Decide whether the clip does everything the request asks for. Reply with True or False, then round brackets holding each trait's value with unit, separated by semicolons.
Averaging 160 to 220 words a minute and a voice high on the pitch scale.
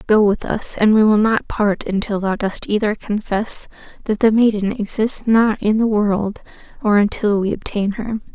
True (185 wpm; 210 Hz)